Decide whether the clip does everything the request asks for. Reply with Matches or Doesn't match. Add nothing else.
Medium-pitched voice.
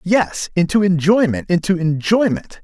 Matches